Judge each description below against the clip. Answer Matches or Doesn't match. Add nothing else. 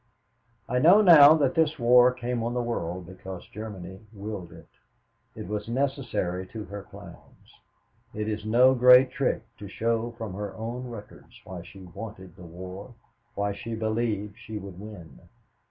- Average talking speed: Matches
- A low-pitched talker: Matches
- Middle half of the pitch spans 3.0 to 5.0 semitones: Matches